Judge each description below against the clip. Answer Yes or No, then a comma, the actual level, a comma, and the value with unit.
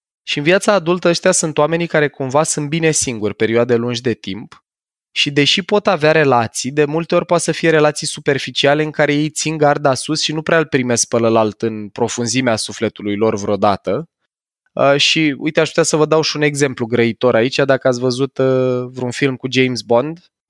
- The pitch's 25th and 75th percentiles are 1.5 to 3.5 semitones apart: No, average, 4.6 semitones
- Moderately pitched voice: Yes, medium, 145 Hz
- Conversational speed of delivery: No, fast, 195 wpm